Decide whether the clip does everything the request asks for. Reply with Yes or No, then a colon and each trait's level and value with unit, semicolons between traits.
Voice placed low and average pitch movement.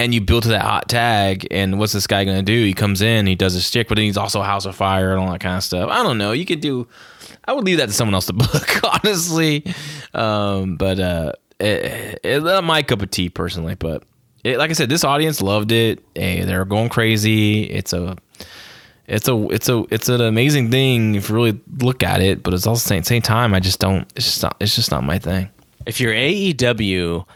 Yes: low, 105 Hz; average, 4.2 semitones